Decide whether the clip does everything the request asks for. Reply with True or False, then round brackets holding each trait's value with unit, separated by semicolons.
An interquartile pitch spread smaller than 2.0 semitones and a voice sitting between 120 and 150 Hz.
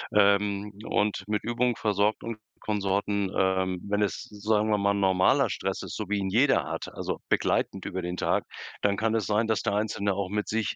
False (1.5 semitones; 105 Hz)